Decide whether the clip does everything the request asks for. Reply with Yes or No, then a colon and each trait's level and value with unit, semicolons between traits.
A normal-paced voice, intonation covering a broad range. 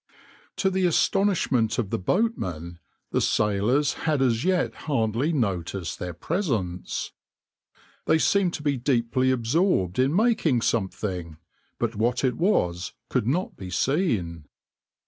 No: slow, 130 wpm; wide, 8.7 semitones